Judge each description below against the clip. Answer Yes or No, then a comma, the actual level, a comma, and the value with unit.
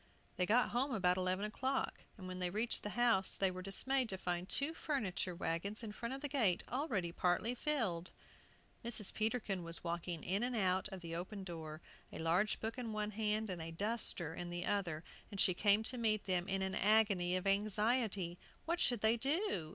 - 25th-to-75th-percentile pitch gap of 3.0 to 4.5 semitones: Yes, average, 4.1 semitones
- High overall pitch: Yes, high, 200 Hz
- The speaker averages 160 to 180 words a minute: No, average, 195 wpm